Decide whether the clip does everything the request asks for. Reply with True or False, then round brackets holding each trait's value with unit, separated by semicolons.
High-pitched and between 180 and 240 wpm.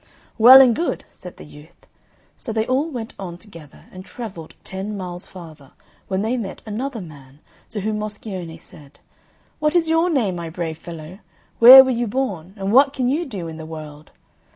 True (200 Hz; 185 wpm)